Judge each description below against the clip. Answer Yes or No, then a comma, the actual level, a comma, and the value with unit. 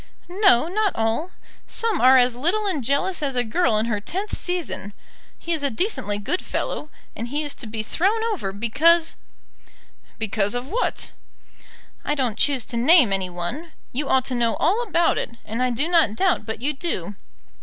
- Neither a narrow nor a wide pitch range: No, wide, 7.3 semitones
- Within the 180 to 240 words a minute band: Yes, average, 190 wpm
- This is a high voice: Yes, very high, 270 Hz